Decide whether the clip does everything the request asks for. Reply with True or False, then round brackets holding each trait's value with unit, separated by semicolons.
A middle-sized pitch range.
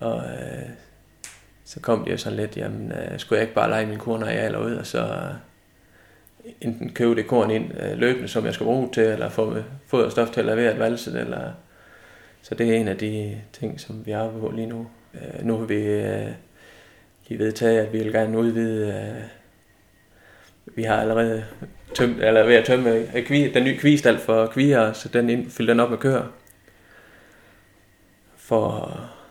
False (1.7 semitones)